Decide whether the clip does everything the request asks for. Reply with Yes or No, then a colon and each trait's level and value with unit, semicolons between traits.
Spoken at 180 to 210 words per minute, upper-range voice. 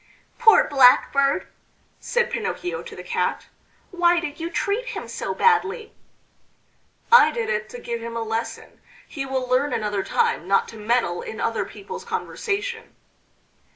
No: average, 150 wpm; very high, 290 Hz